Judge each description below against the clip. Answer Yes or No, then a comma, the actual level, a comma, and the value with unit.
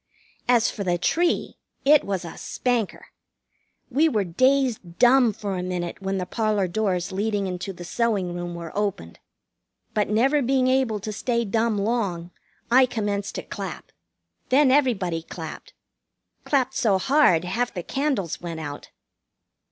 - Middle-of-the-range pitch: No, high, 210 Hz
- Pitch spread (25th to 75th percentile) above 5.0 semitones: Yes, wide, 5.6 semitones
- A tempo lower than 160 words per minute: Yes, average, 150 wpm